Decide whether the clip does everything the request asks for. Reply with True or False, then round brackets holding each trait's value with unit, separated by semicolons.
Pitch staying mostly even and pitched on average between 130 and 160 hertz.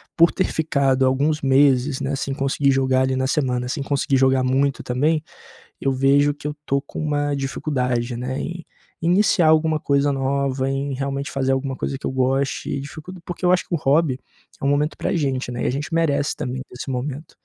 True (2.1 semitones; 140 Hz)